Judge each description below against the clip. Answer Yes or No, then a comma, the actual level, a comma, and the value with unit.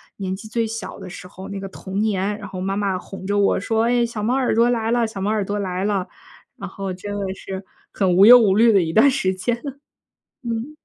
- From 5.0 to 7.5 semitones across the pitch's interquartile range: No, average, 3.0 semitones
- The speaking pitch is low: No, high, 205 Hz